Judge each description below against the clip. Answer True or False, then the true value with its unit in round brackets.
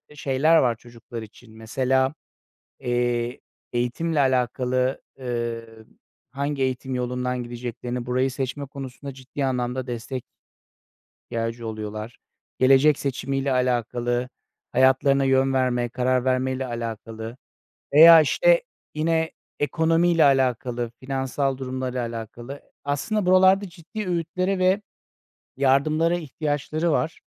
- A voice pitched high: False (130 Hz)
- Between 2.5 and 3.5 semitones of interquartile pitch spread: True (3.0 semitones)